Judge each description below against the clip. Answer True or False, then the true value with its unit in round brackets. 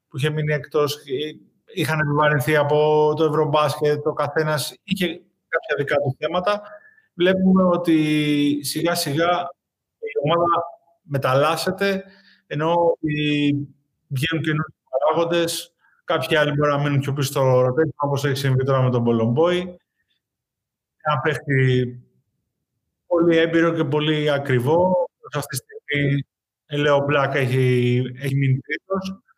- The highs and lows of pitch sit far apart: False (3.1 semitones)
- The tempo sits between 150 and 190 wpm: False (125 wpm)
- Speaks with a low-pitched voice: False (150 Hz)